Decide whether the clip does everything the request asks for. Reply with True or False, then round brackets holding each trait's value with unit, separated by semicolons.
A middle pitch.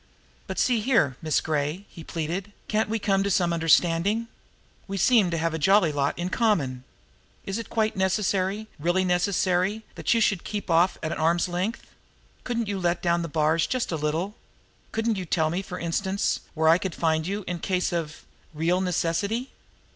True (180 Hz)